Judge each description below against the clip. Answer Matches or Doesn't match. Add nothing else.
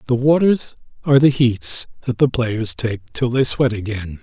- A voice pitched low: Matches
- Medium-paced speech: Matches